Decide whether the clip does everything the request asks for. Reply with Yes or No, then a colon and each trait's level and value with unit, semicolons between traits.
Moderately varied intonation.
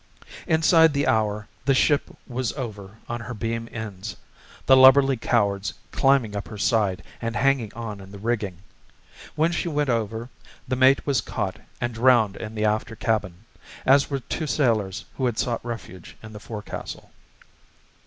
Yes: average, 3.9 semitones